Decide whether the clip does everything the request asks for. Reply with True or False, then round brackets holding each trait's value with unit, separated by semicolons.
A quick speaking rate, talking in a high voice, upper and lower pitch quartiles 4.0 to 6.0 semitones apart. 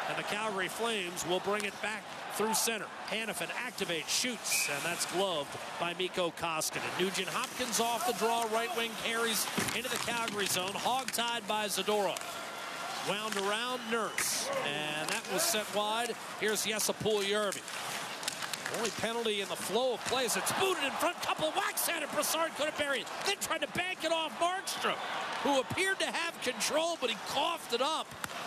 False (175 wpm; 225 Hz; 4.3 semitones)